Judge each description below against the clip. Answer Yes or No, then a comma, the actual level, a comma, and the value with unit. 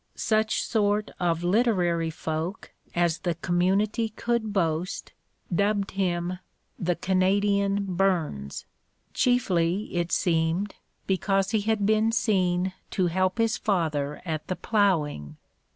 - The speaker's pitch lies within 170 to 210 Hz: Yes, medium, 185 Hz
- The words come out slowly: Yes, slow, 115 wpm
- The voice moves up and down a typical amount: Yes, average, 3.3 semitones